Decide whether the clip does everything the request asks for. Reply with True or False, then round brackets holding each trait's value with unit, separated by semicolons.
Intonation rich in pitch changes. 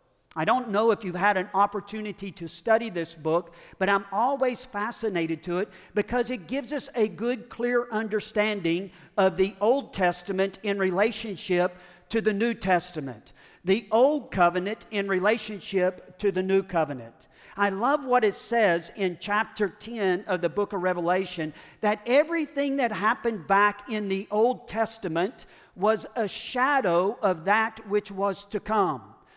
False (3.4 semitones)